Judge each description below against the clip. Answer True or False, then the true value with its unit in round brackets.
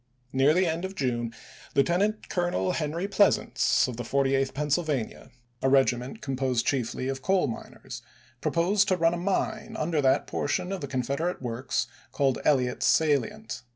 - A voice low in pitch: False (145 Hz)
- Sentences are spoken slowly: False (155 wpm)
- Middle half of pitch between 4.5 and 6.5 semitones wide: True (5.2 semitones)